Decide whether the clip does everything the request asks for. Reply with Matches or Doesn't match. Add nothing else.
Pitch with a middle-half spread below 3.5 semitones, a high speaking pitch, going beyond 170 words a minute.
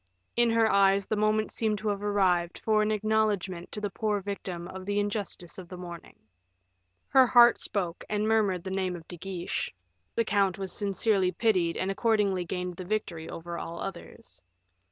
Matches